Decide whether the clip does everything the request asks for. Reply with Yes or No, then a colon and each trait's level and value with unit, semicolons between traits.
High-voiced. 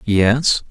No: low, 110 Hz